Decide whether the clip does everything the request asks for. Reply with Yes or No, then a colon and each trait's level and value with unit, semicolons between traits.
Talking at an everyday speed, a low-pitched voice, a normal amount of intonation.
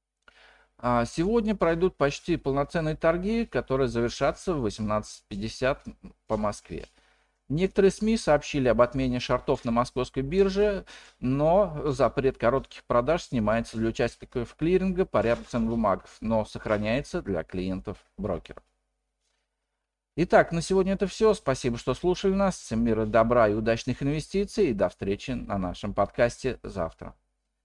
No: average, 125 wpm; low, 130 Hz; wide, 7.4 semitones